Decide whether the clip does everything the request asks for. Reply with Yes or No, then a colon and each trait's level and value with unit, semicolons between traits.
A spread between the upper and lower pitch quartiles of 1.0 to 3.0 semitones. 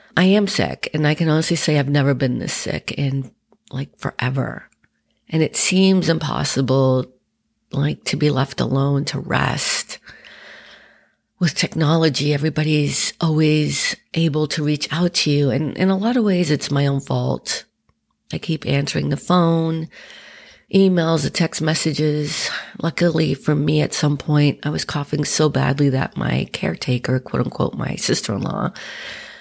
Yes: average, 2.7 semitones